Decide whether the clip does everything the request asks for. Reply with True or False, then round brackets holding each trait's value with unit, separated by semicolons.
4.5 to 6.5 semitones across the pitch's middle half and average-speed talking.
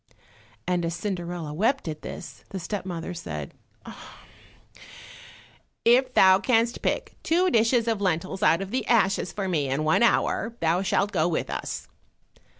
True (5.3 semitones; 150 wpm)